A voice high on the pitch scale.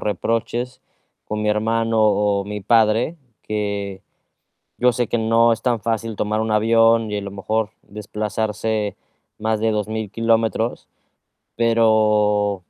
No: low, 110 Hz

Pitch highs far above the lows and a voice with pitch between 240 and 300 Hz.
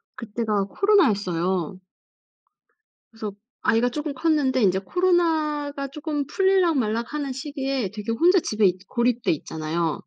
Yes: wide, 6.7 semitones; very high, 250 Hz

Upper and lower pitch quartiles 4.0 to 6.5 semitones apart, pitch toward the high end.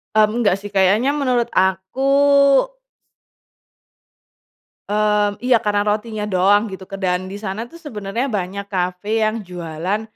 No: average, 2.7 semitones; high, 205 Hz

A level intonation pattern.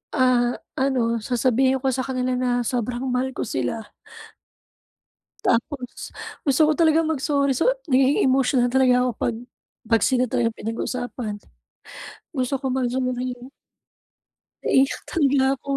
Yes: narrow, 1.7 semitones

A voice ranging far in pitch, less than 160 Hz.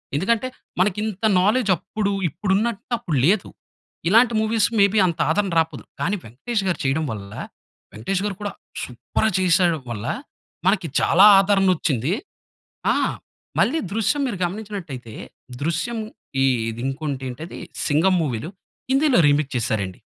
No: wide, 6.4 semitones; medium, 185 Hz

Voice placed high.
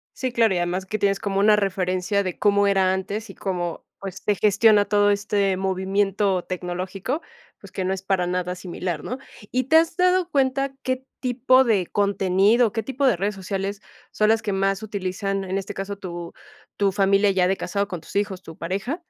Yes: high, 200 Hz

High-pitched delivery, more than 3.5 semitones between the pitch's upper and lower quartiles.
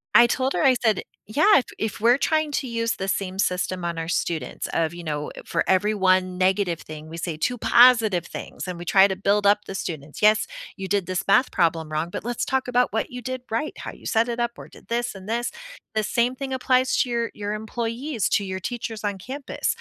Yes: high, 210 Hz; average, 4.6 semitones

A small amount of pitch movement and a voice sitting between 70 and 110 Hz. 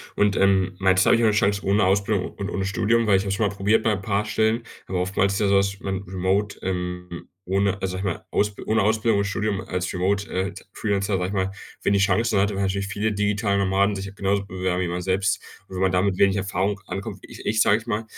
Yes: narrow, 1.5 semitones; low, 100 Hz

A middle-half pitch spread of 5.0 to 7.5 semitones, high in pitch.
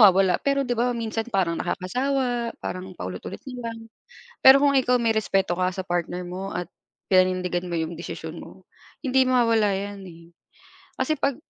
Yes: average, 5.3 semitones; high, 205 Hz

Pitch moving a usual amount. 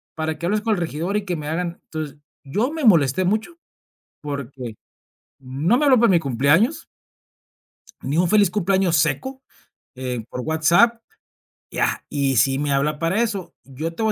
No: wide, 6.7 semitones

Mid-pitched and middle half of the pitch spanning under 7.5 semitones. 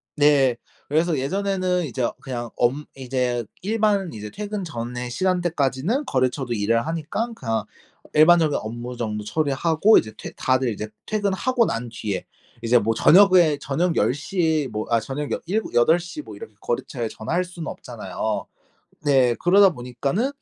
Yes: medium, 145 Hz; wide, 7.0 semitones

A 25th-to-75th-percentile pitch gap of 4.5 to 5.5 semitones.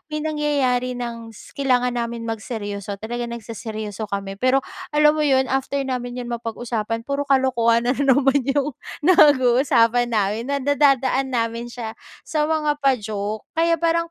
No: average, 3.5 semitones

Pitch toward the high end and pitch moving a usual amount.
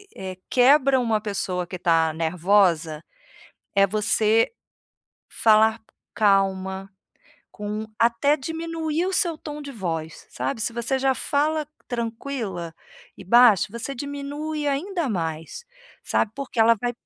No: high, 225 Hz; wide, 6.7 semitones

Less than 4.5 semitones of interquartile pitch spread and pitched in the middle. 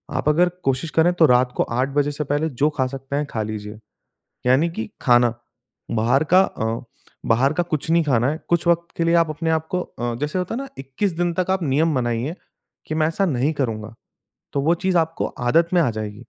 No: average, 5.2 semitones; medium, 145 Hz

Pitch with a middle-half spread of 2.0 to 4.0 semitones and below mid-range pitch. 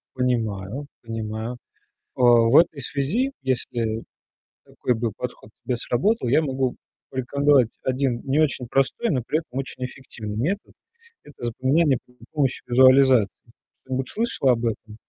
Yes: average, 2.9 semitones; low, 130 Hz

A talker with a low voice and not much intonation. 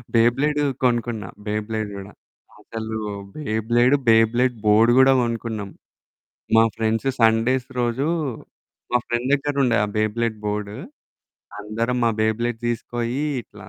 Yes: low, 115 Hz; narrow, 2.0 semitones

